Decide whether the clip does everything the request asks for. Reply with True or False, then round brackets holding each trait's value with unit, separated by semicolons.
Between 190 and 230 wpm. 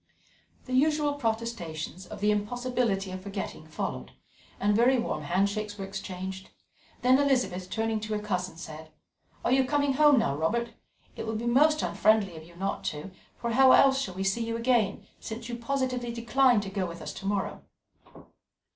False (175 wpm)